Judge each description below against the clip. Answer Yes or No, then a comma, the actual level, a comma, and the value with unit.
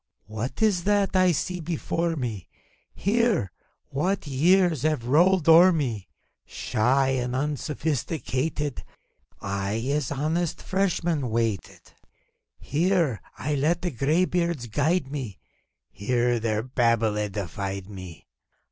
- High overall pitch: No, medium, 145 Hz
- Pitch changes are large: Yes, wide, 6.7 semitones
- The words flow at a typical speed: No, slow, 110 wpm